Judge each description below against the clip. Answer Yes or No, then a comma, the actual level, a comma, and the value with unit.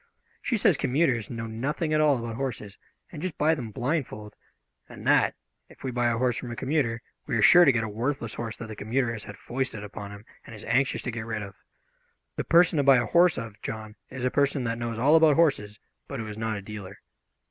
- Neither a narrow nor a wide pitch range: Yes, average, 4.2 semitones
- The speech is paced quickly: Yes, fast, 235 wpm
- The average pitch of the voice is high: No, low, 120 Hz